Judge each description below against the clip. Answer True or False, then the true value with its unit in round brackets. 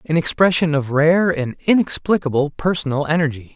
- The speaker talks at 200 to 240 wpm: False (135 wpm)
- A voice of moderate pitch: True (155 Hz)